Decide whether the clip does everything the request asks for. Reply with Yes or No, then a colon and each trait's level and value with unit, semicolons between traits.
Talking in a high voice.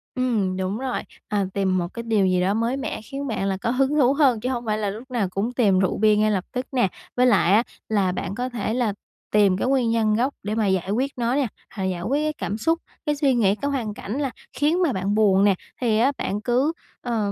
Yes: high, 220 Hz